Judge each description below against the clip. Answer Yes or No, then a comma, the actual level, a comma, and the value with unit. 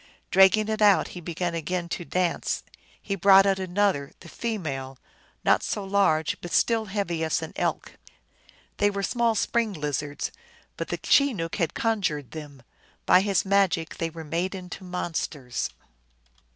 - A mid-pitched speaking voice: Yes, medium, 180 Hz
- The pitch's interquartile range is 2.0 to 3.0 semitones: No, average, 3.8 semitones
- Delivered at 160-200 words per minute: No, average, 150 wpm